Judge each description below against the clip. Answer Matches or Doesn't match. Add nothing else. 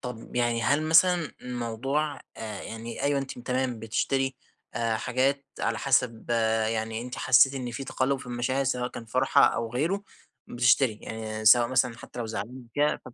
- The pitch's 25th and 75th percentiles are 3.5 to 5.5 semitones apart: Doesn't match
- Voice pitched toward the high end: Doesn't match